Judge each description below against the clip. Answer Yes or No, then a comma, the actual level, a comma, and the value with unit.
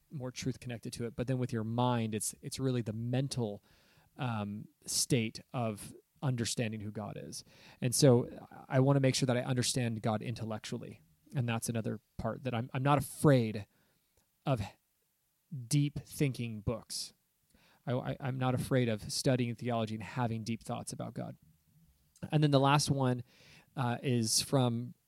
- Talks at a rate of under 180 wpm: Yes, average, 165 wpm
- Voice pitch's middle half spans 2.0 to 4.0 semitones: Yes, average, 2.9 semitones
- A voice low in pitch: Yes, low, 125 Hz